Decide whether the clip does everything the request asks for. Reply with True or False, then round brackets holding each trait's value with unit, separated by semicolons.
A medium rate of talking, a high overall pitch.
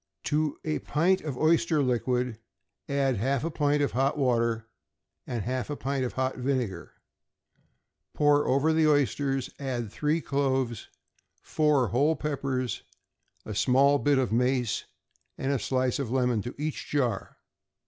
False (145 wpm; 135 Hz)